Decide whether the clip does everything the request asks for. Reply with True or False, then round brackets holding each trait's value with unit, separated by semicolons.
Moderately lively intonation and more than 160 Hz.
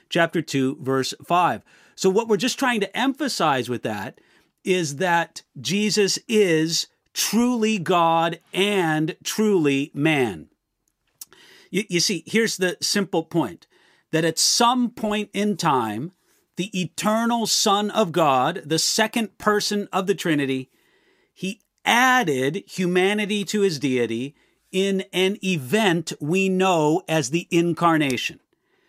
True (4.3 semitones; 185 Hz)